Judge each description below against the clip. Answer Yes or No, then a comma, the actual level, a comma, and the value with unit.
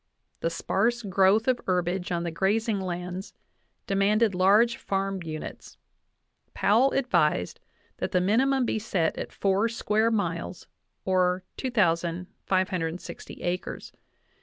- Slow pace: Yes, slow, 110 wpm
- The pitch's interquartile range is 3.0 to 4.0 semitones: Yes, average, 3.5 semitones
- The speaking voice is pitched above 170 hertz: Yes, high, 190 Hz